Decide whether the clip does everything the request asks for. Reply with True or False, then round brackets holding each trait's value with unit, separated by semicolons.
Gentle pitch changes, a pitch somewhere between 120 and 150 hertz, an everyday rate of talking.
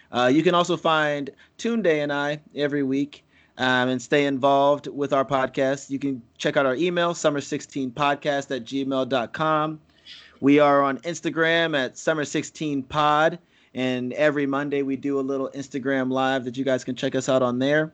True (2.1 semitones; 140 Hz; 170 wpm)